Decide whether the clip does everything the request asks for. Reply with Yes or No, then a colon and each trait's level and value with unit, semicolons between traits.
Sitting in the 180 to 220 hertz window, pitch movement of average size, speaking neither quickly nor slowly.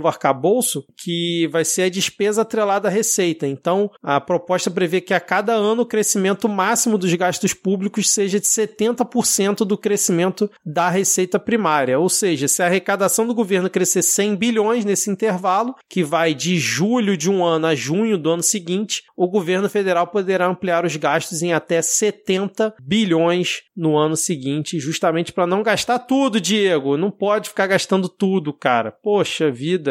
Yes: high, 190 Hz; average, 3.4 semitones; average, 165 wpm